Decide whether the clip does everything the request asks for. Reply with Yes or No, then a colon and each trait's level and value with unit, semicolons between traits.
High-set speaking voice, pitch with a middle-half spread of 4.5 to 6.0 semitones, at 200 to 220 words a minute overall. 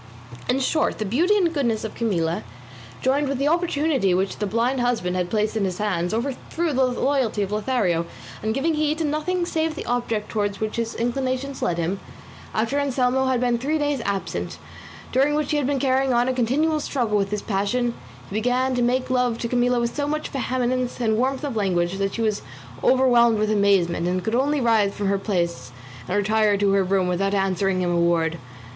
Yes: high, 235 Hz; average, 5.0 semitones; fast, 205 wpm